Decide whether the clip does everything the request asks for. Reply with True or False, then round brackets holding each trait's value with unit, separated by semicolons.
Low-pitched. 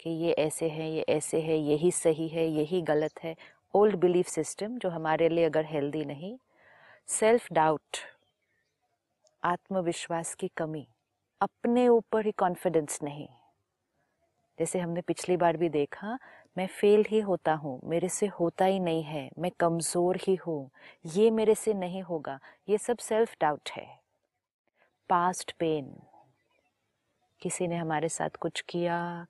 False (170 Hz)